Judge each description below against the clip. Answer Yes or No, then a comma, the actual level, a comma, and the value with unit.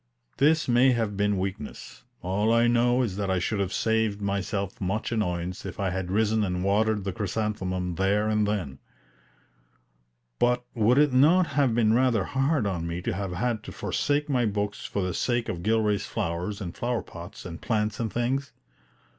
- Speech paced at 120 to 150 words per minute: No, average, 180 wpm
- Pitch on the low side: Yes, low, 105 Hz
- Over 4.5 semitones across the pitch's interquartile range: No, average, 3.8 semitones